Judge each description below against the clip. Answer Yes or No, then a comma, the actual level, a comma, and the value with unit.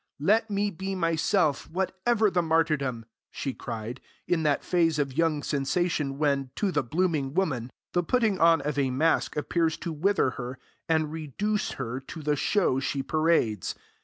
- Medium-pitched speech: Yes, medium, 160 Hz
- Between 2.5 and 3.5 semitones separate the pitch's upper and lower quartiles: No, average, 4.6 semitones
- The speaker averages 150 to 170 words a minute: Yes, average, 160 wpm